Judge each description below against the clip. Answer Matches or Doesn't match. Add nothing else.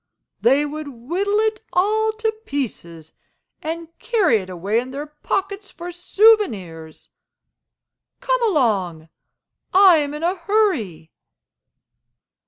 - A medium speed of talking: Doesn't match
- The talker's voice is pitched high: Matches